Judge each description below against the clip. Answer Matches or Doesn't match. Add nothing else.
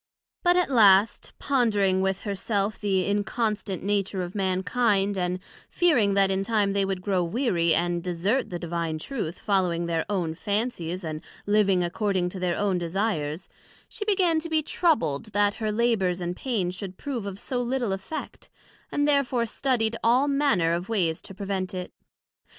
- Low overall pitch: Doesn't match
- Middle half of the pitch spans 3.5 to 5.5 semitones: Matches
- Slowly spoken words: Doesn't match